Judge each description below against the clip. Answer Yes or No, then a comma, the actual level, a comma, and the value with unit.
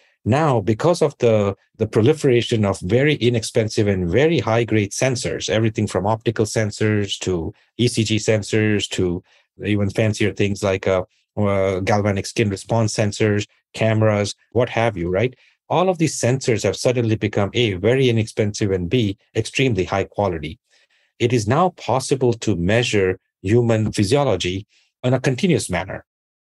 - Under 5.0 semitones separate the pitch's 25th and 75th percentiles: Yes, average, 3.2 semitones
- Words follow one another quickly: No, average, 145 wpm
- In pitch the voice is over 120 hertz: No, low, 110 Hz